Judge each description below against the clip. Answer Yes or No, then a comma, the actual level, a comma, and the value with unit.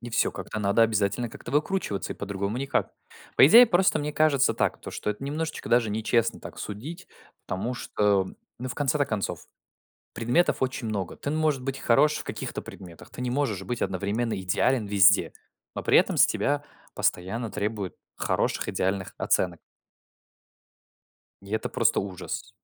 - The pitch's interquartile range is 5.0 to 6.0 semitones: Yes, wide, 5.5 semitones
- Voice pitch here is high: No, low, 115 Hz